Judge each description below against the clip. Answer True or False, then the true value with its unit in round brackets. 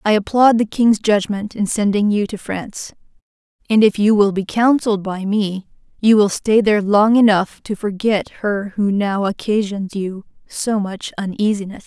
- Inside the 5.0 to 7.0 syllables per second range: False (4.6 syllables/s)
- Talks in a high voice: True (205 Hz)